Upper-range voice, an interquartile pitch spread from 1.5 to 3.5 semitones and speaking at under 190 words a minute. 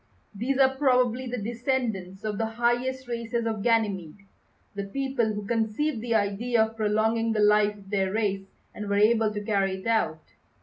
Yes: high, 220 Hz; average, 2.7 semitones; average, 175 wpm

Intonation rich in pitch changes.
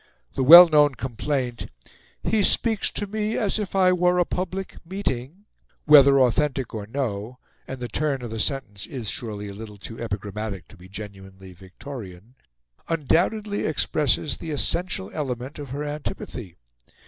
Yes: wide, 7.3 semitones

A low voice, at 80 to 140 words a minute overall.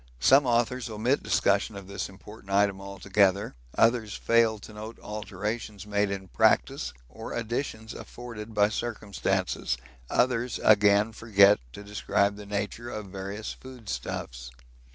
Yes: low, 105 Hz; slow, 135 wpm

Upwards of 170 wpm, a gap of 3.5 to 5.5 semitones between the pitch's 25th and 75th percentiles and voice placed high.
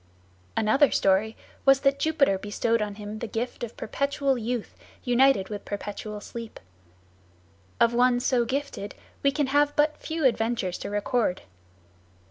No: average, 140 wpm; average, 4.5 semitones; high, 240 Hz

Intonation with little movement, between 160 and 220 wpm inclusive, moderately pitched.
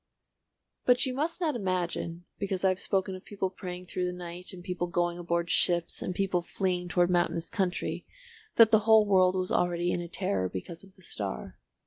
Yes: narrow, 1.9 semitones; average, 195 wpm; medium, 180 Hz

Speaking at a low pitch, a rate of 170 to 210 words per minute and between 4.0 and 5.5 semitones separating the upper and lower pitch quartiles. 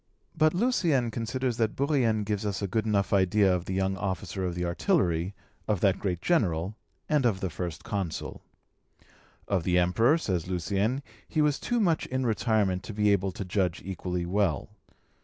Yes: low, 100 Hz; average, 175 wpm; average, 4.7 semitones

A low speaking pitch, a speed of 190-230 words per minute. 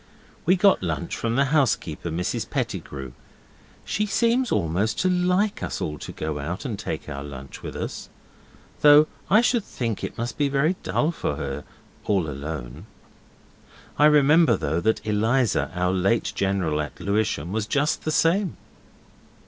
No: low, 110 Hz; average, 155 wpm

